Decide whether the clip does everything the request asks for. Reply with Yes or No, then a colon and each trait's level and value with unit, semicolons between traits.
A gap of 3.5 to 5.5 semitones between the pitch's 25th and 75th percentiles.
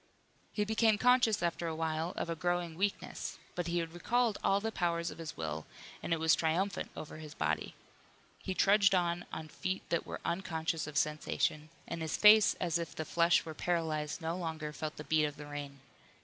No: average, 2.9 semitones